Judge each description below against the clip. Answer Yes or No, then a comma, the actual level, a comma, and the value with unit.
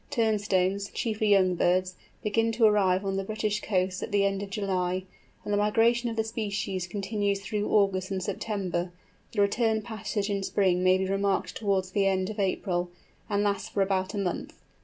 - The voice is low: No, high, 200 Hz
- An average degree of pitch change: No, narrow, 2.1 semitones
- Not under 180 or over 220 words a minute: Yes, average, 185 wpm